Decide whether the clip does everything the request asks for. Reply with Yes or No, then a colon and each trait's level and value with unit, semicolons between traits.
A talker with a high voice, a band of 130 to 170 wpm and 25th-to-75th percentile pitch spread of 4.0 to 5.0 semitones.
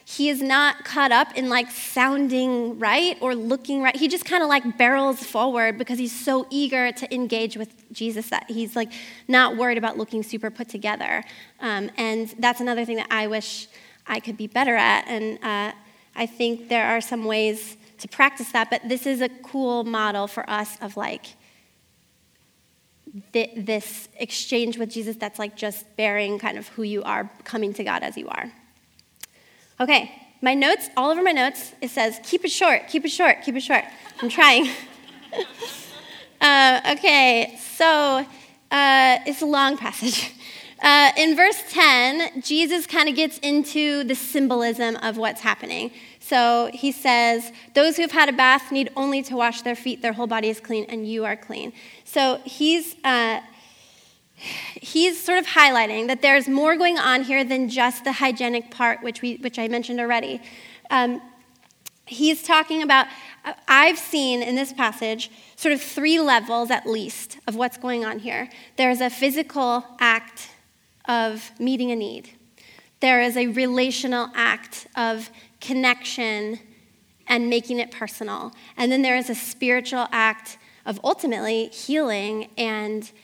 No: high, 245 Hz; average, 165 wpm; average, 3.1 semitones